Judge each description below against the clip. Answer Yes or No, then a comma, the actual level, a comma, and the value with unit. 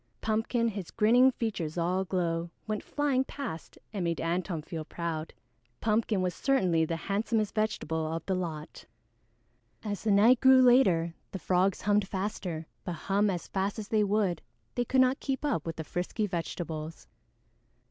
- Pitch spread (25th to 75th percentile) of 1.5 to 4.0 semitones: No, average, 4.7 semitones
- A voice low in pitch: No, high, 195 Hz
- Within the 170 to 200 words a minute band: No, average, 160 wpm